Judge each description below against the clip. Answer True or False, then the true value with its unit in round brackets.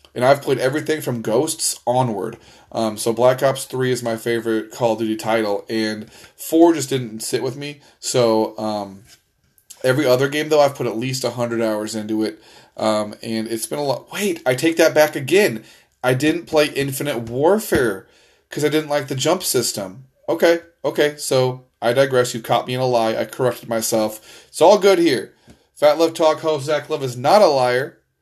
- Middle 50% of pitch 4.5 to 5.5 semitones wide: True (5.0 semitones)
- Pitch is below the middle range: True (130 Hz)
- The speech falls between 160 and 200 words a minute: True (195 wpm)